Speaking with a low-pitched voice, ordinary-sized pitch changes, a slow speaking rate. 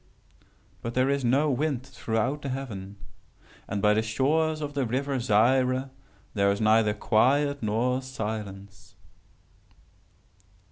Yes: low, 125 Hz; average, 4.2 semitones; slow, 125 wpm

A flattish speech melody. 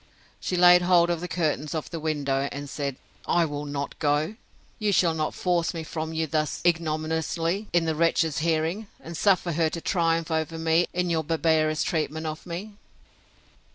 Yes: narrow, 1.8 semitones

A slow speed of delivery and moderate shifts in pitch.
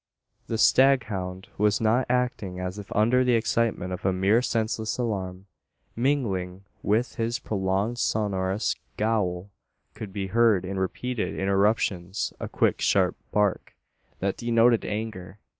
Yes: slow, 130 wpm; average, 3.5 semitones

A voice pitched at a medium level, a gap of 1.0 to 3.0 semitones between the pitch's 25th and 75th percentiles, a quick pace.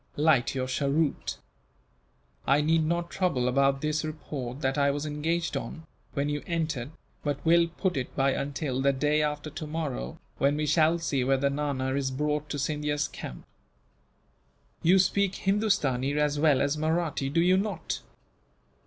No: medium, 150 Hz; average, 2.7 semitones; average, 155 wpm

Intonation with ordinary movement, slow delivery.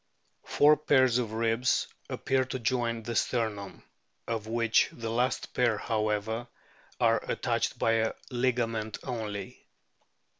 No: narrow, 2.0 semitones; slow, 120 wpm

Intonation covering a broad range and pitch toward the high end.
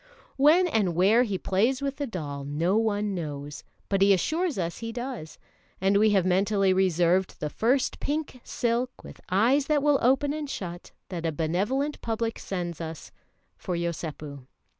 Yes: wide, 6.8 semitones; high, 200 Hz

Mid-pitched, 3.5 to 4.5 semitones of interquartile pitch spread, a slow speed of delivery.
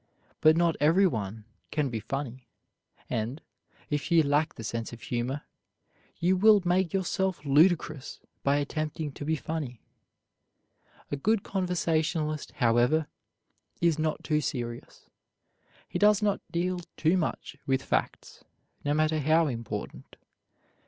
Yes: medium, 155 Hz; average, 4.1 semitones; slow, 125 wpm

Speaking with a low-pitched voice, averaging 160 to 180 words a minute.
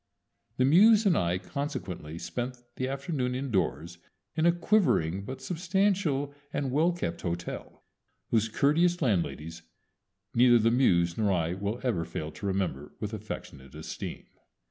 No: low, 115 Hz; average, 140 wpm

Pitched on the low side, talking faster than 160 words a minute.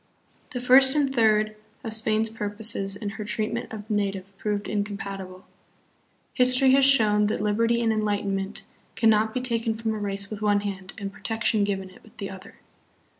No: high, 215 Hz; average, 175 wpm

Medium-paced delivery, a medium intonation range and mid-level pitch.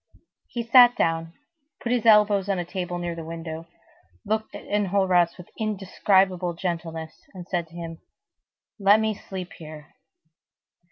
Yes: average, 145 wpm; average, 3.7 semitones; medium, 180 Hz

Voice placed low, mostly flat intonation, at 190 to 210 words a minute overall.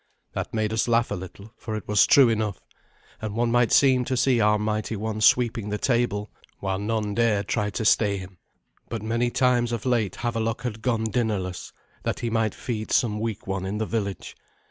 Yes: low, 110 Hz; narrow, 2.2 semitones; average, 200 wpm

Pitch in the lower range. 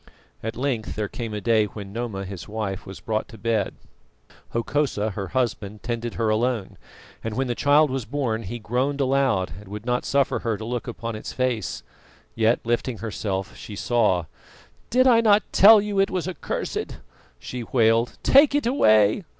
Yes: low, 115 Hz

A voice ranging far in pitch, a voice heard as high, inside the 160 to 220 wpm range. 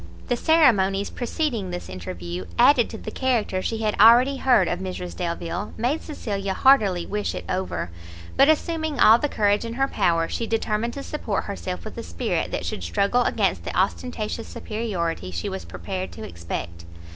Yes: wide, 6.6 semitones; high, 205 Hz; average, 175 wpm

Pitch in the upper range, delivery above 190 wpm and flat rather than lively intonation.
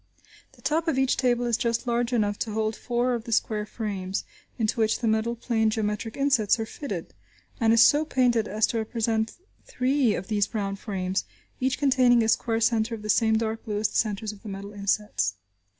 Yes: high, 225 Hz; fast, 205 wpm; narrow, 2.3 semitones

